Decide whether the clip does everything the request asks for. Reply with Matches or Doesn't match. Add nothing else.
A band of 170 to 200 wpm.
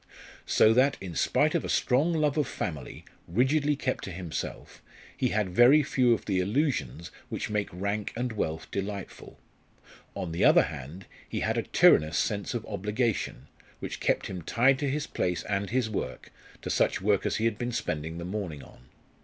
Matches